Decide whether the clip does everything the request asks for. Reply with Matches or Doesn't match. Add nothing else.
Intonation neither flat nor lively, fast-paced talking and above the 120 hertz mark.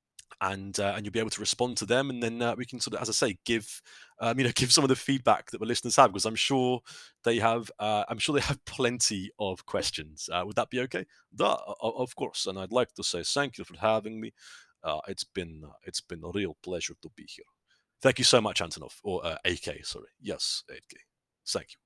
Doesn't match